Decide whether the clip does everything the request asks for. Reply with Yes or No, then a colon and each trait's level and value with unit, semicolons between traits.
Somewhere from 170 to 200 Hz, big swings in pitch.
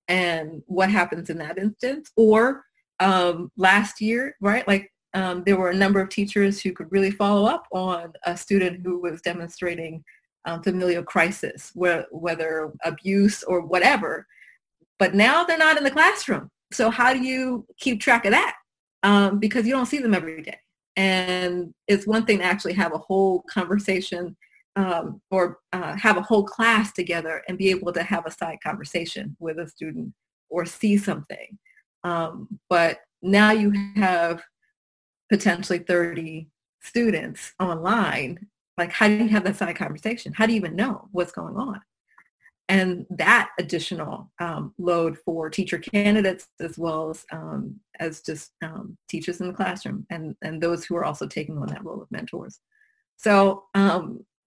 No: high, 190 Hz; average, 3.2 semitones